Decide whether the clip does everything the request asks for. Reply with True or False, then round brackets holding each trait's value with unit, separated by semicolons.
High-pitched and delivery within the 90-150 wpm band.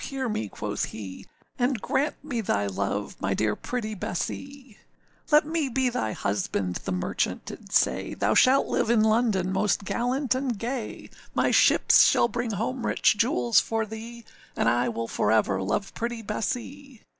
False (225 Hz; 170 wpm)